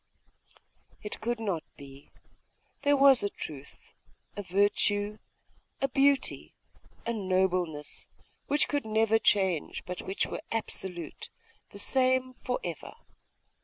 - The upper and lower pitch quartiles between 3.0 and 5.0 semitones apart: No, wide, 5.5 semitones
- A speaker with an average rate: No, slow, 115 wpm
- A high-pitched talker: Yes, high, 205 Hz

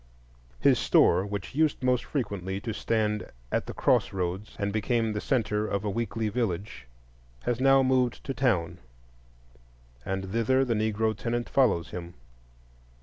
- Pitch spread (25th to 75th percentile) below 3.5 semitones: No, average, 3.8 semitones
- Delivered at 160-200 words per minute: No, average, 145 wpm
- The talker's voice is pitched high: No, low, 110 Hz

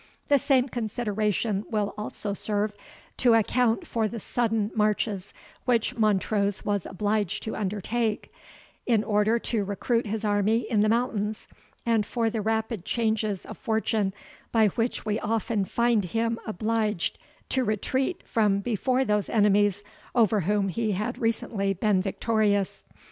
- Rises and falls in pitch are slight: Yes, narrow, 1.9 semitones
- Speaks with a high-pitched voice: Yes, high, 215 Hz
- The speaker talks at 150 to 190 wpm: No, average, 140 wpm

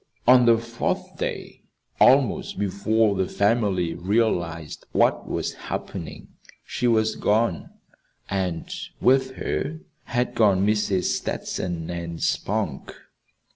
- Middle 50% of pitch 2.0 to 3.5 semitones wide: No, average, 4.3 semitones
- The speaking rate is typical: No, slow, 105 wpm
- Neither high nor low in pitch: No, low, 105 Hz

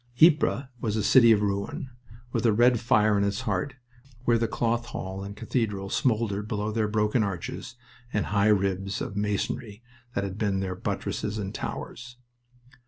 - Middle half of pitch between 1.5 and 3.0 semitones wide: Yes, average, 2.7 semitones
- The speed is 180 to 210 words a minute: No, average, 170 wpm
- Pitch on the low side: Yes, low, 105 Hz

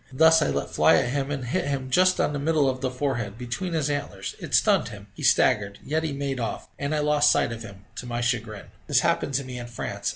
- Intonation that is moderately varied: Yes, average, 3.5 semitones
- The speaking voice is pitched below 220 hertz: Yes, low, 135 Hz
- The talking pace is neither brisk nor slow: No, fast, 255 wpm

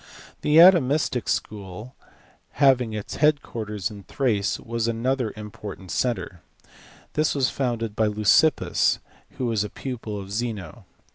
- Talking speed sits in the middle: No, slow, 130 wpm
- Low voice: Yes, low, 115 Hz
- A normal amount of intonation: Yes, average, 3.9 semitones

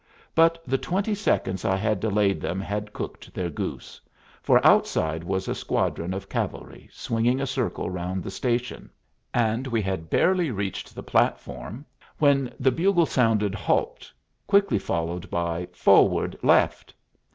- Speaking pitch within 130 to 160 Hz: No, low, 105 Hz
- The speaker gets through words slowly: No, average, 145 wpm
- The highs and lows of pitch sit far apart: Yes, wide, 6.2 semitones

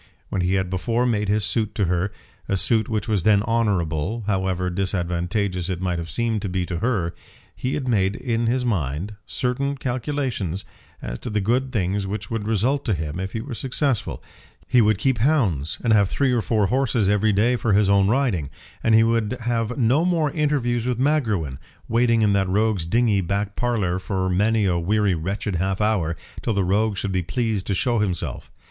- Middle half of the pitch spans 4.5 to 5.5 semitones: No, average, 4.0 semitones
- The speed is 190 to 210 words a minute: Yes, average, 200 wpm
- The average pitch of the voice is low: Yes, low, 105 Hz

